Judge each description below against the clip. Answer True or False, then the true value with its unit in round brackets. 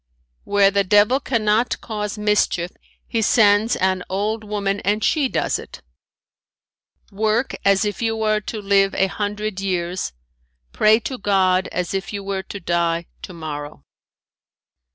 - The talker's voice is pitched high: True (205 Hz)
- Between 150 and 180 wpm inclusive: False (140 wpm)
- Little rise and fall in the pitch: True (2.1 semitones)